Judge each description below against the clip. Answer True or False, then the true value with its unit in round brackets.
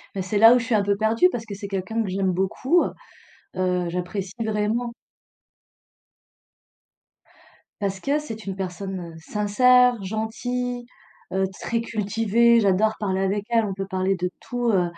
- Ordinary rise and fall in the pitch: True (3.3 semitones)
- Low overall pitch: False (205 Hz)